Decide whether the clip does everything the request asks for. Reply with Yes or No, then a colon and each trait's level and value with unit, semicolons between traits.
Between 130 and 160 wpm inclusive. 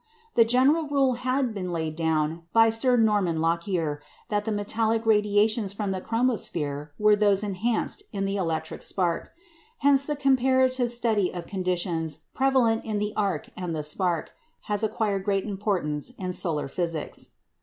Yes: average, 155 wpm